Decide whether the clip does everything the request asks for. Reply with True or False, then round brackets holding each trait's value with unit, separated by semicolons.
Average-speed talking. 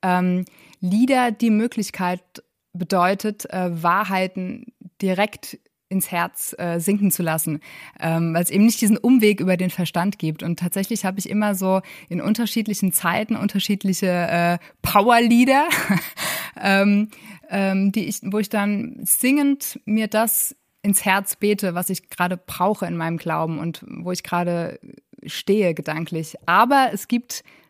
True (145 wpm)